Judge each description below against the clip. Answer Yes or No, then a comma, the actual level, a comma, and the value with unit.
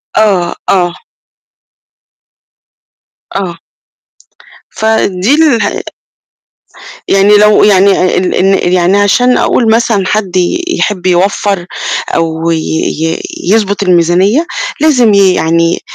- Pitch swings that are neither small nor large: Yes, average, 3.4 semitones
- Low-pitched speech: No, high, 195 Hz